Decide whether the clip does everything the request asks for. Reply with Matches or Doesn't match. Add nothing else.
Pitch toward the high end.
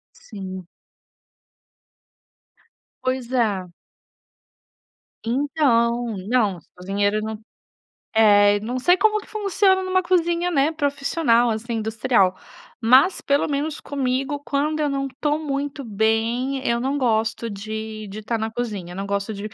Matches